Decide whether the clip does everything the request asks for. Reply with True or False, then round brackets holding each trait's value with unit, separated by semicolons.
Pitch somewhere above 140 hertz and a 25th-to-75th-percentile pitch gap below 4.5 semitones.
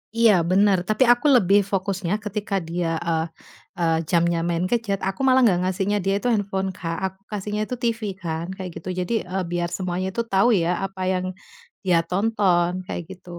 True (190 Hz; 2.9 semitones)